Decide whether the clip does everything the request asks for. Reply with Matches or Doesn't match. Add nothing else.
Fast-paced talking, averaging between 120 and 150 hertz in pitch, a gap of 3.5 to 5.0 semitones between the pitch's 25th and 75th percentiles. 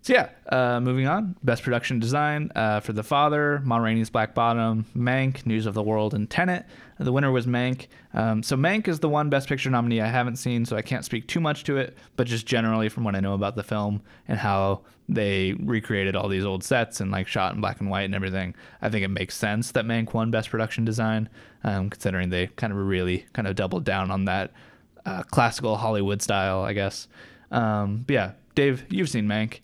Doesn't match